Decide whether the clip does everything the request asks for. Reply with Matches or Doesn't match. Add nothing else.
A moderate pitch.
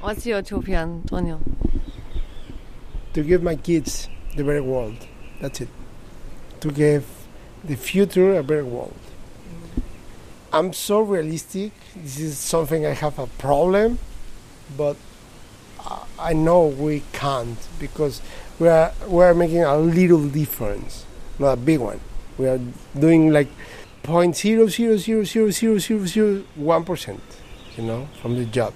Matches